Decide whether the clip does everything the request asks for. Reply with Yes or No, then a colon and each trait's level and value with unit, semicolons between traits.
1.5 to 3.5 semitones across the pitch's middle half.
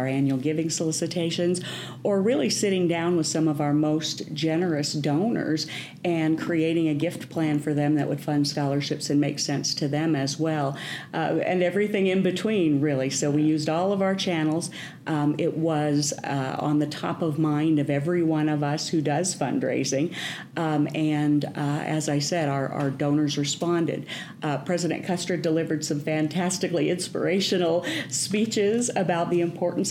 Yes: average, 2.8 semitones